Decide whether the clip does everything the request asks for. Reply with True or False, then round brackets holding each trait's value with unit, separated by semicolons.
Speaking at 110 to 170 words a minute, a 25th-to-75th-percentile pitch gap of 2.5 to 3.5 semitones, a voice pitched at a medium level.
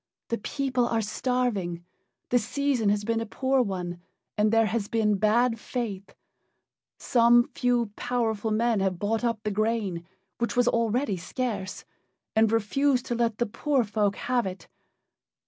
False (150 wpm; 2.9 semitones; 225 Hz)